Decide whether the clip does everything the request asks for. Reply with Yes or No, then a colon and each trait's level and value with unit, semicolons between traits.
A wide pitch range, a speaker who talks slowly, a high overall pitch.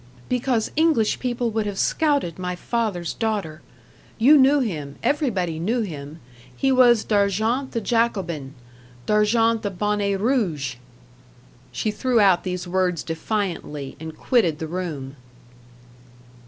Yes: wide, 5.7 semitones; slow, 125 wpm; high, 205 Hz